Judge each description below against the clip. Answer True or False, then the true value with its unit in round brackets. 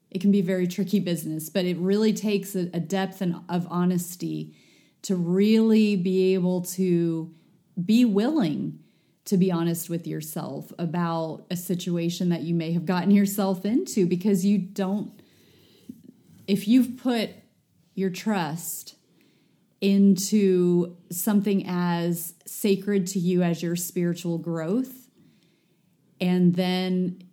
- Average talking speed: False (125 wpm)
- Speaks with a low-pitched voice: False (180 Hz)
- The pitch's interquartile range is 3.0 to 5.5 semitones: False (2.5 semitones)